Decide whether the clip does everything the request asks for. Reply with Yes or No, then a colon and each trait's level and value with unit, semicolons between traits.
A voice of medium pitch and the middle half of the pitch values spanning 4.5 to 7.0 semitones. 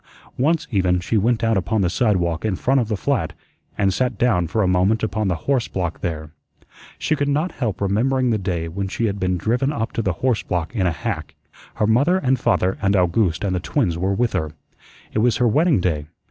No: low, 100 Hz; average, 5.1 semitones